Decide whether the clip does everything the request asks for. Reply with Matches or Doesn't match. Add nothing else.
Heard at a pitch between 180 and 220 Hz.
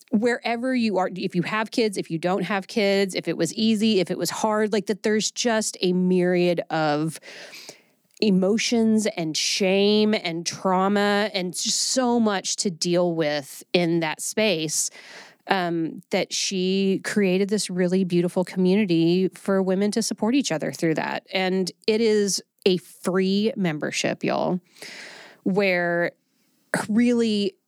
Matches